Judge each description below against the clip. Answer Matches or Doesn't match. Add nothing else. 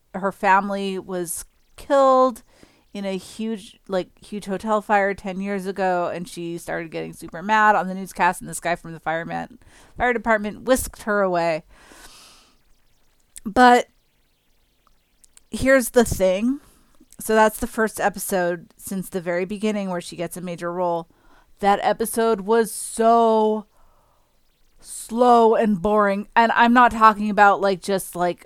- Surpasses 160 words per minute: Doesn't match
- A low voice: Doesn't match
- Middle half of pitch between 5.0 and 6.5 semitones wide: Doesn't match